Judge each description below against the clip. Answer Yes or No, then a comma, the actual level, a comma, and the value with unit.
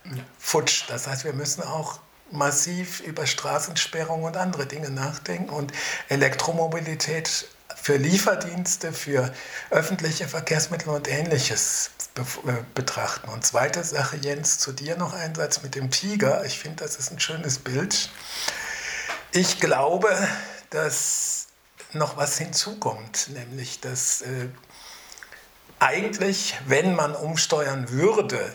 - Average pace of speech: No, slow, 120 wpm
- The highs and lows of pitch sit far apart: No, average, 3.7 semitones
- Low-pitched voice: No, medium, 150 Hz